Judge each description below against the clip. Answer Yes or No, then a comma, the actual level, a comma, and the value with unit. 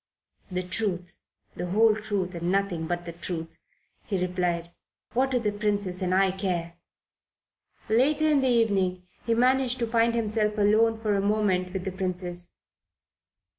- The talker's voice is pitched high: Yes, high, 195 Hz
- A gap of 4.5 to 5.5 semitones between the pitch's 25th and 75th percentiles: No, average, 3.7 semitones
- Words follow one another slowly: No, average, 155 wpm